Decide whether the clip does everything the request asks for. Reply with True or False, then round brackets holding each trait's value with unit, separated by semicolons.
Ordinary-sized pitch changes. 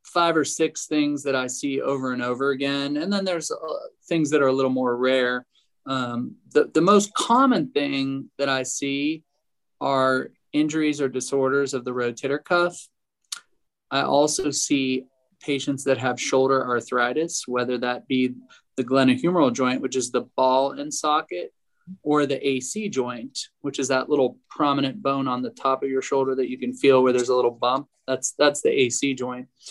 False (2.3 semitones)